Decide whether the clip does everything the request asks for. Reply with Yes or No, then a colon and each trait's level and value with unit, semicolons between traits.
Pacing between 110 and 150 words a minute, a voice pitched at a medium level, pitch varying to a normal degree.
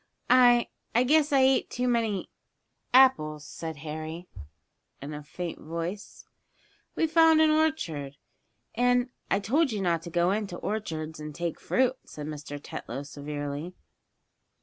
No: average, 145 wpm; medium, 180 Hz; wide, 8.4 semitones